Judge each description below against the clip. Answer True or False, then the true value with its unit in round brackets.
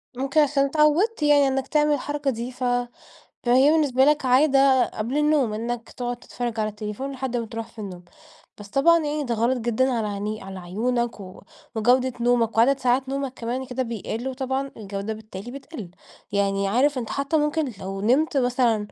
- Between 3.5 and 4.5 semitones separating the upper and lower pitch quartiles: True (3.8 semitones)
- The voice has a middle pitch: False (250 Hz)